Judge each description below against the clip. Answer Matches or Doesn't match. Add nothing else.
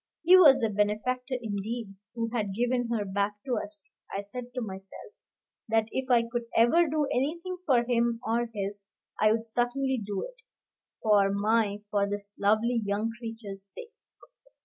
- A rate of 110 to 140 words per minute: Doesn't match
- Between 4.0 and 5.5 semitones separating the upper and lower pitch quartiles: Doesn't match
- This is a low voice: Doesn't match